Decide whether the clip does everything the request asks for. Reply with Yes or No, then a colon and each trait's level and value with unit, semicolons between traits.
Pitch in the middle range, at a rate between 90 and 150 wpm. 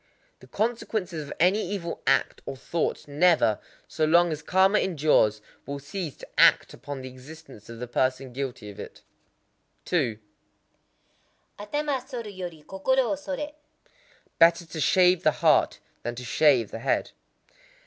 Yes: medium, 160 Hz; average, 140 wpm